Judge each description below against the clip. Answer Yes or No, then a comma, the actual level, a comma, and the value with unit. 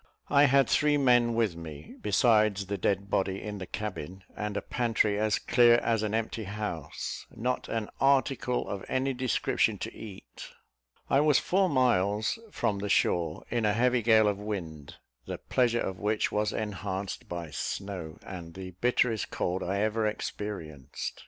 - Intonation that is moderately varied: Yes, average, 3.7 semitones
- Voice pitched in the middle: No, low, 105 Hz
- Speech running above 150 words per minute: Yes, average, 165 wpm